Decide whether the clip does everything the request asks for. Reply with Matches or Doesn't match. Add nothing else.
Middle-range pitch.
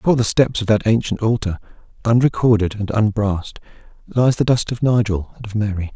Doesn't match